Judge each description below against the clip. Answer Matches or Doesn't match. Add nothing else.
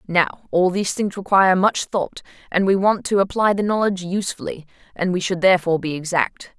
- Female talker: Matches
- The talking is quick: Doesn't match